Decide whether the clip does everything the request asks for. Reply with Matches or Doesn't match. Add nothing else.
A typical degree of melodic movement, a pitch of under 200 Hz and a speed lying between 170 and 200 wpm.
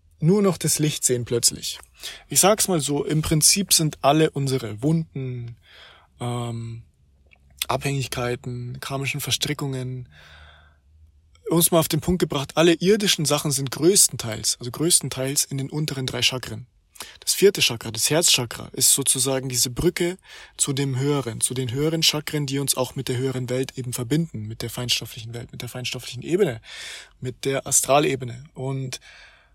Doesn't match